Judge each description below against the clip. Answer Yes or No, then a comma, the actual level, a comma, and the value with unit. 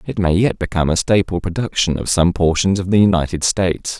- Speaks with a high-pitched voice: No, very low, 90 Hz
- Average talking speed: No, fast, 210 wpm